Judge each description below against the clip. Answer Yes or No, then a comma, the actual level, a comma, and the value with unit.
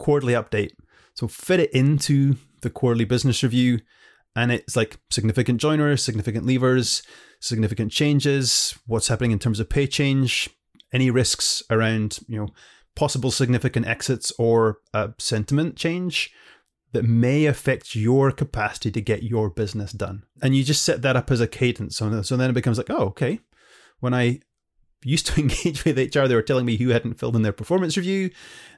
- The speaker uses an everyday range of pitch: Yes, average, 3.4 semitones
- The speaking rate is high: No, average, 175 wpm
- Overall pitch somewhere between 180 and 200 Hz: No, low, 125 Hz